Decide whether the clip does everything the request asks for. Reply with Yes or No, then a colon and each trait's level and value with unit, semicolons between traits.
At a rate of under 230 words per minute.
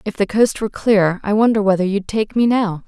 No: fast, 250 wpm